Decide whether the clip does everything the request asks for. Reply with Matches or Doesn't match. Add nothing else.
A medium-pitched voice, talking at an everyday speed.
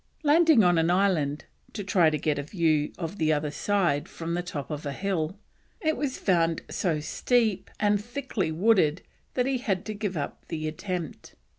Matches